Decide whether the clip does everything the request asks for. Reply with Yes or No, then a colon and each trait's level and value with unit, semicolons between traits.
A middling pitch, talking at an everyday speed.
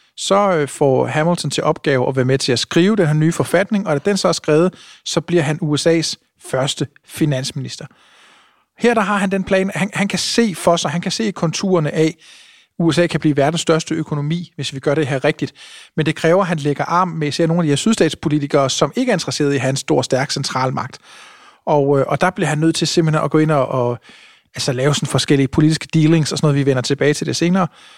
No: medium, 160 Hz; fast, 230 wpm